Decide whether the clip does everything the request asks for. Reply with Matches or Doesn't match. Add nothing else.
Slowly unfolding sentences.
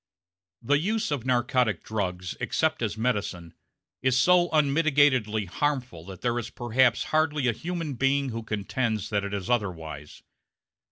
Doesn't match